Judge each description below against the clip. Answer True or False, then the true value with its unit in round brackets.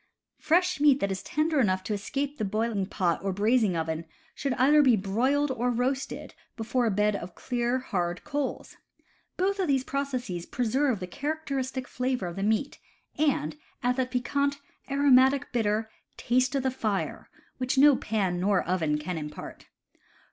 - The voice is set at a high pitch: True (245 Hz)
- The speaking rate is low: False (170 wpm)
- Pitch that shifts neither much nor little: False (5.8 semitones)